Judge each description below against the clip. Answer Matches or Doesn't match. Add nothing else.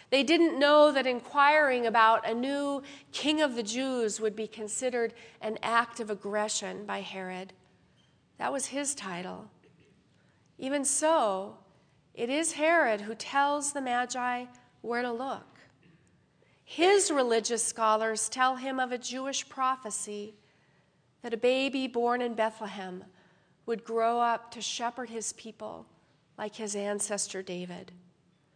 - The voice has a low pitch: Doesn't match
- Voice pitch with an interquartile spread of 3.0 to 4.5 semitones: Matches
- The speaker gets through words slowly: Matches